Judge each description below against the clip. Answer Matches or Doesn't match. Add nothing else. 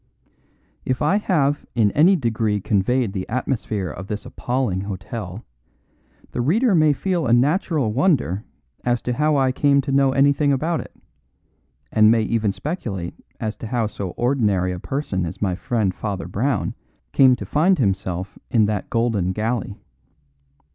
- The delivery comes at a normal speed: Matches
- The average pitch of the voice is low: Matches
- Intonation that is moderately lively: Doesn't match